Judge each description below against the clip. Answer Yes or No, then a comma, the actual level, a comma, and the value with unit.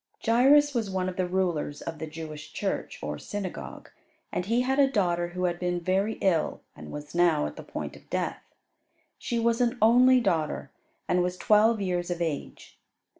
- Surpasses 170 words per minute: Yes, average, 185 wpm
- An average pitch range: Yes, average, 5.0 semitones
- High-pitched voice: No, medium, 180 Hz